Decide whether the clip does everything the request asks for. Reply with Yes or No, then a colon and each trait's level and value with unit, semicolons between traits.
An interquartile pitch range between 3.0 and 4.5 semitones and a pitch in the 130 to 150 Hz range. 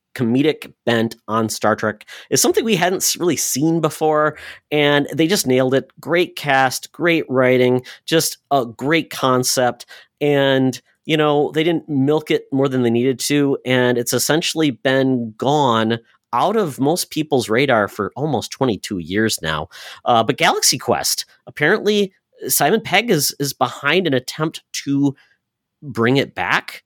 Yes: average, 3.7 semitones; medium, 140 Hz